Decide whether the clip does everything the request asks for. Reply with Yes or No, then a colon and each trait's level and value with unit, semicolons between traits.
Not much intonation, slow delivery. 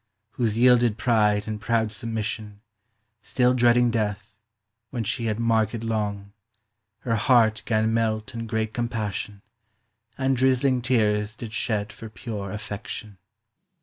Yes: narrow, 2.1 semitones; slow, 125 wpm